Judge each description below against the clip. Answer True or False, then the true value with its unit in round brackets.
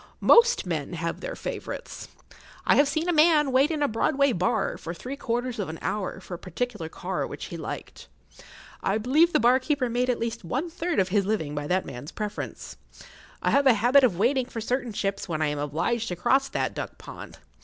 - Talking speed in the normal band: False (215 wpm)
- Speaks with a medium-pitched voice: False (235 Hz)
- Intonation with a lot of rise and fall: True (7.1 semitones)